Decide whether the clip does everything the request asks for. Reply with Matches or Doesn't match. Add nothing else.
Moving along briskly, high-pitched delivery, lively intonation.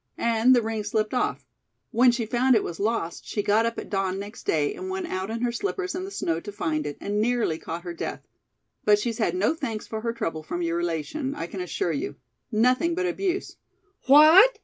Matches